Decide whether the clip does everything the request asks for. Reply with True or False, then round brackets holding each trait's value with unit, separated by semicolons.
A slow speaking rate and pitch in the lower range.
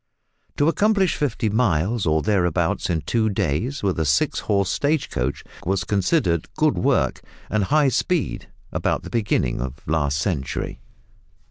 False (145 wpm; 100 Hz)